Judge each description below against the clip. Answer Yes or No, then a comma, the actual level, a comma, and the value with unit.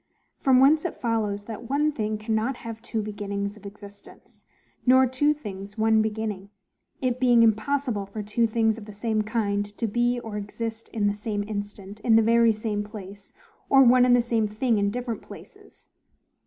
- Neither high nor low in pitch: No, high, 220 Hz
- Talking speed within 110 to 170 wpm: No, average, 180 wpm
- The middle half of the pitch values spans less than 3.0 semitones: Yes, narrow, 2.6 semitones